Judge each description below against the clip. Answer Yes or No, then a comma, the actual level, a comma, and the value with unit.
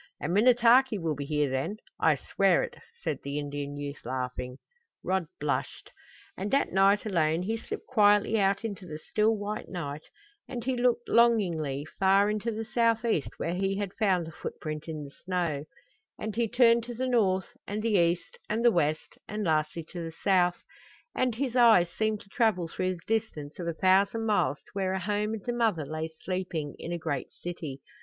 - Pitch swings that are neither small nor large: No, wide, 5.7 semitones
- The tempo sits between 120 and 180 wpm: No, average, 190 wpm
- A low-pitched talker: No, high, 190 Hz